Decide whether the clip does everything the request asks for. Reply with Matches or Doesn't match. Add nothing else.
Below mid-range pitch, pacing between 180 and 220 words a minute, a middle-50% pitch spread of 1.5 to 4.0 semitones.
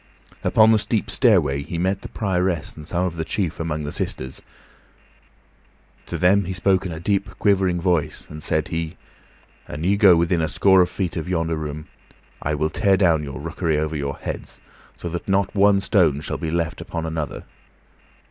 Matches